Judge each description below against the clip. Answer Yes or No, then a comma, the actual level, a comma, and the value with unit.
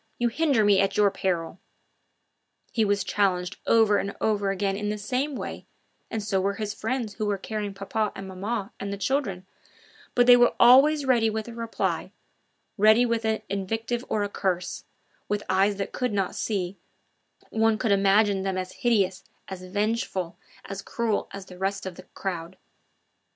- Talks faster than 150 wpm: Yes, average, 175 wpm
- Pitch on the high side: Yes, high, 205 Hz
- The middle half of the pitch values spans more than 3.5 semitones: No, narrow, 2.6 semitones